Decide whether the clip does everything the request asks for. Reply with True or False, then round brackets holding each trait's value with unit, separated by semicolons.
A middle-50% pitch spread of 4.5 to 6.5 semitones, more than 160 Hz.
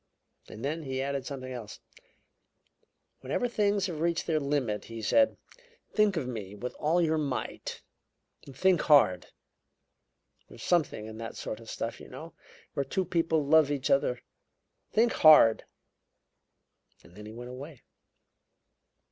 False (5.5 semitones; 145 Hz)